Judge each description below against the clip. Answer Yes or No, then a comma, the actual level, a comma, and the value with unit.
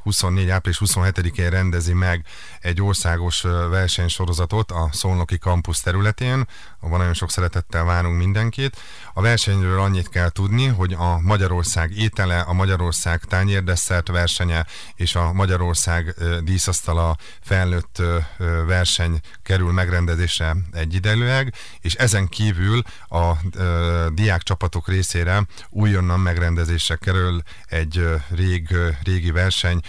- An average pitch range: No, narrow, 1.8 semitones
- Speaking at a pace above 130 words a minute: No, average, 110 wpm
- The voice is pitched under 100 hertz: Yes, very low, 90 Hz